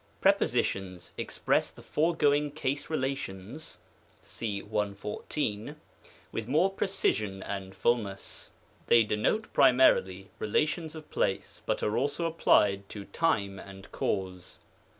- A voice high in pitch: No, low, 110 Hz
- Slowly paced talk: Yes, slow, 110 wpm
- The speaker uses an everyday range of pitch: No, wide, 7.1 semitones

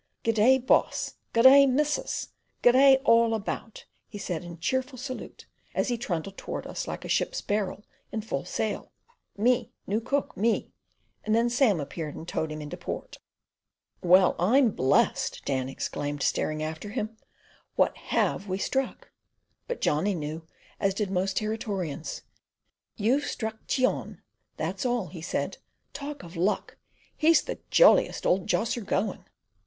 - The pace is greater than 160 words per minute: No, average, 150 wpm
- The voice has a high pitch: Yes, high, 215 Hz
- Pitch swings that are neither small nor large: No, wide, 6.0 semitones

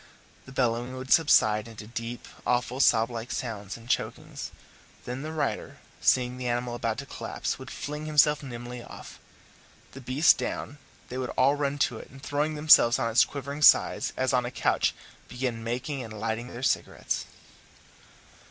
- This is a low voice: Yes, low, 125 Hz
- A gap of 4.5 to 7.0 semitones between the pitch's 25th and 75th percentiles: No, average, 3.0 semitones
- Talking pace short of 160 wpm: No, average, 170 wpm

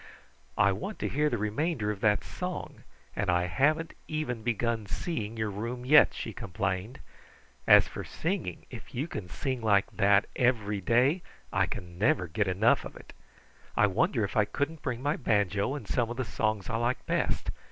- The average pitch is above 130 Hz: No, low, 110 Hz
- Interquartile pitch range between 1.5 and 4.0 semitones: No, average, 4.4 semitones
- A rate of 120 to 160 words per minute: No, average, 185 wpm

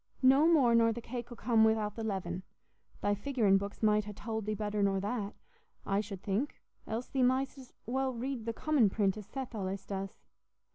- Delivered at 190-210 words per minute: Yes, average, 200 wpm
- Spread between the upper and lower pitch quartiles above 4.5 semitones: No, average, 3.6 semitones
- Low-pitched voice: No, high, 220 Hz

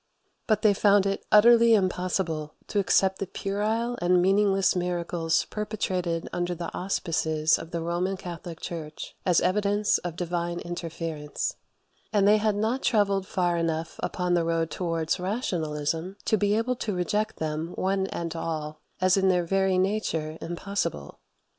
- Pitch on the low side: No, medium, 180 Hz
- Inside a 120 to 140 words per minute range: No, average, 150 wpm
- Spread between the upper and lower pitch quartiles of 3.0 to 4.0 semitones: Yes, average, 3.3 semitones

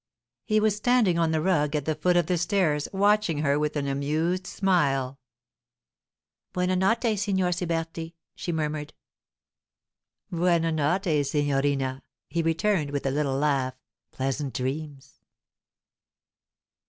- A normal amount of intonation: Yes, average, 4.1 semitones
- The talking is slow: Yes, slow, 125 wpm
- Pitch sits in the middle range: Yes, medium, 160 Hz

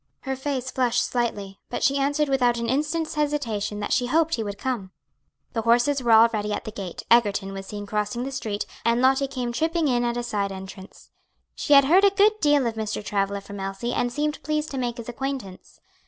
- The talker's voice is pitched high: Yes, high, 240 Hz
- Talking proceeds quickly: Yes, fast, 215 wpm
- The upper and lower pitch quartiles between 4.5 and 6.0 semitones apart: Yes, average, 4.9 semitones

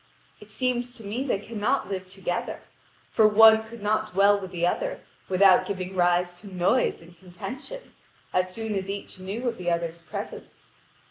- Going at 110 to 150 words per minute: No, average, 175 wpm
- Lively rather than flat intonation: No, average, 3.4 semitones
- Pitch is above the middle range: Yes, high, 200 Hz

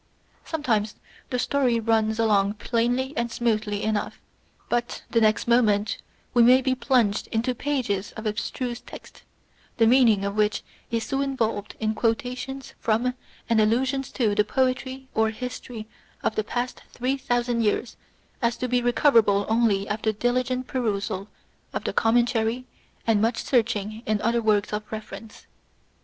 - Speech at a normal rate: Yes, average, 145 wpm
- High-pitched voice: Yes, high, 230 Hz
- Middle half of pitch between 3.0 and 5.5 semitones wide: No, narrow, 2.6 semitones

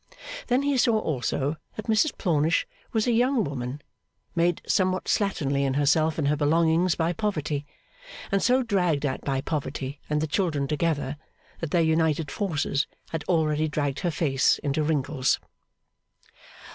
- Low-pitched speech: No, medium, 155 Hz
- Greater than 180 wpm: No, average, 150 wpm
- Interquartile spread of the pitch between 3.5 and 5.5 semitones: Yes, average, 4.3 semitones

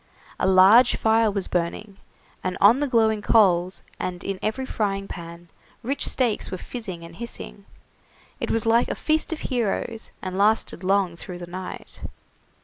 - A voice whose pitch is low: No, high, 200 Hz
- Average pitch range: Yes, average, 3.7 semitones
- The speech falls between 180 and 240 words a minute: No, average, 160 wpm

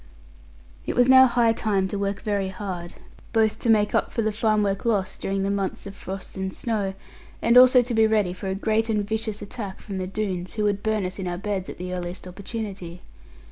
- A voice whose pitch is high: Yes, high, 205 Hz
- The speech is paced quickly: Yes, fast, 220 wpm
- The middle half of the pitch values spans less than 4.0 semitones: Yes, narrow, 2.5 semitones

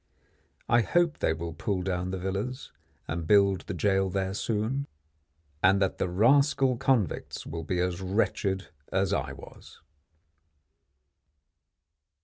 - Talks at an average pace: No, slow, 125 wpm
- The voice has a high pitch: No, very low, 95 Hz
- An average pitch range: Yes, average, 3.5 semitones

